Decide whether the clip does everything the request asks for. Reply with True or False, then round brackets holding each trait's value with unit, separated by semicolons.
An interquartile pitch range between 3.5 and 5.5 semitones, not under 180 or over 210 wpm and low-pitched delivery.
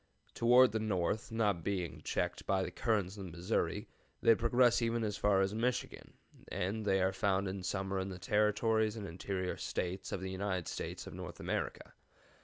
False (2.8 semitones; 185 wpm; 100 Hz)